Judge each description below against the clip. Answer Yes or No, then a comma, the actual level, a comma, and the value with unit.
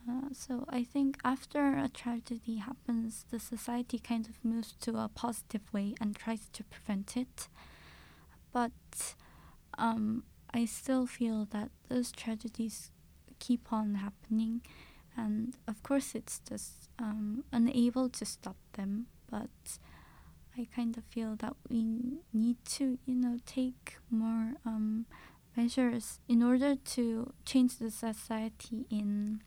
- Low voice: No, high, 235 Hz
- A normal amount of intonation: No, narrow, 2.1 semitones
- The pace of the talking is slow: Yes, slow, 130 wpm